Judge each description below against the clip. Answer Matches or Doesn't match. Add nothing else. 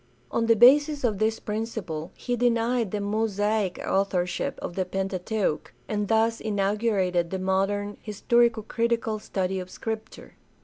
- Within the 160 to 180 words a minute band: Doesn't match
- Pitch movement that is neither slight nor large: Matches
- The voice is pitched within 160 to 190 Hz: Doesn't match